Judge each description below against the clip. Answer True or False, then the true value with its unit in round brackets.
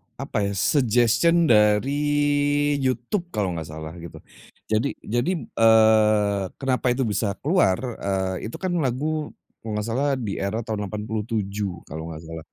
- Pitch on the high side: False (110 Hz)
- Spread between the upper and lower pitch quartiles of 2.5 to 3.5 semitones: False (4.4 semitones)